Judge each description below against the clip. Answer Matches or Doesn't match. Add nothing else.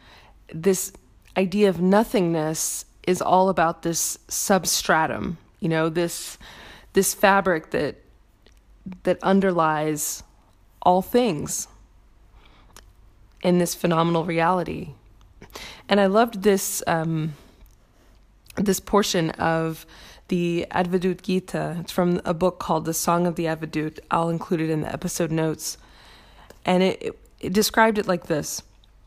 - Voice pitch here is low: Doesn't match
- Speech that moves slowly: Matches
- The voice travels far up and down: Doesn't match